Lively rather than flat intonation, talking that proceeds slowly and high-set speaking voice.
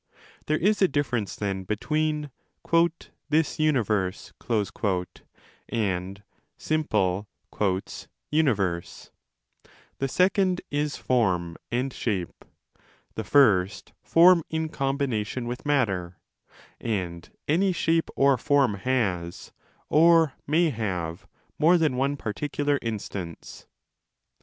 No: wide, 7.6 semitones; slow, 95 wpm; low, 130 Hz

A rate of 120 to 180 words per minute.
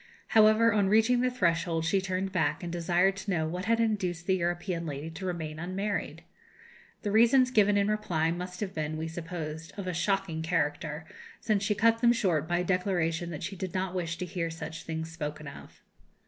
No: average, 200 wpm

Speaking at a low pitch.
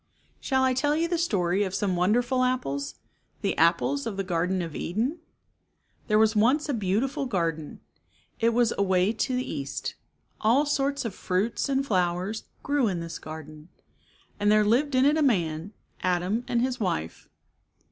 No: high, 210 Hz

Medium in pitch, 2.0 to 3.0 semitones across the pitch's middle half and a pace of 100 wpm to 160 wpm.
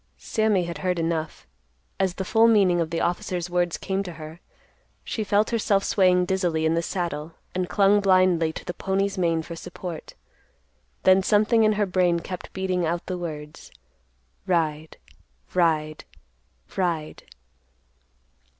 Yes: medium, 180 Hz; narrow, 2.6 semitones; average, 145 wpm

